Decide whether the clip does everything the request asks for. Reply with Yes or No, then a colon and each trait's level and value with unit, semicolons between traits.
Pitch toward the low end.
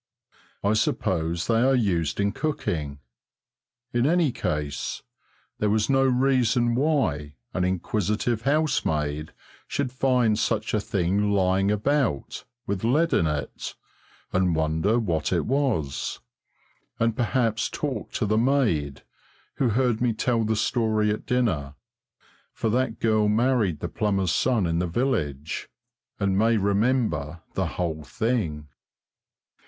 Yes: low, 110 Hz